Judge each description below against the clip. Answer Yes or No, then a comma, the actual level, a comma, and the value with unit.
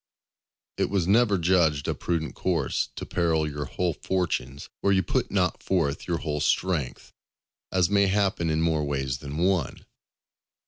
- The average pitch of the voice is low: Yes, very low, 85 Hz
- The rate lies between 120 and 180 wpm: Yes, average, 155 wpm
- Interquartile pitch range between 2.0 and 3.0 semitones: No, average, 4.1 semitones